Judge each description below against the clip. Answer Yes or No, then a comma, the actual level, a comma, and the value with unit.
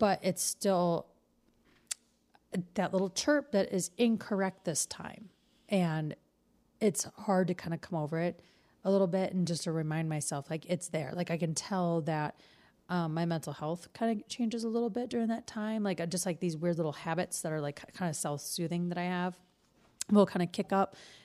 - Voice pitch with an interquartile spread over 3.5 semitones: No, average, 3.1 semitones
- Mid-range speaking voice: Yes, medium, 180 Hz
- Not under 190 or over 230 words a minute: Yes, average, 200 wpm